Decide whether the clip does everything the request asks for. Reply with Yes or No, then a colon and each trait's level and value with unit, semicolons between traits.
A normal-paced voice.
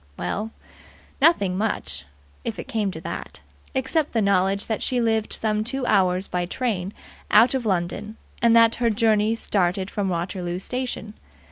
Yes: average, 155 wpm